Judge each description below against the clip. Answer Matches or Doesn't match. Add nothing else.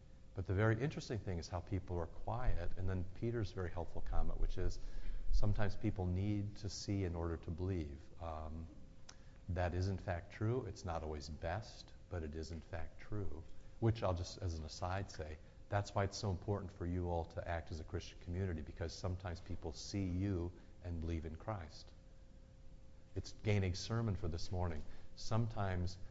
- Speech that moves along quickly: Doesn't match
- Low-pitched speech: Matches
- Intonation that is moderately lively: Matches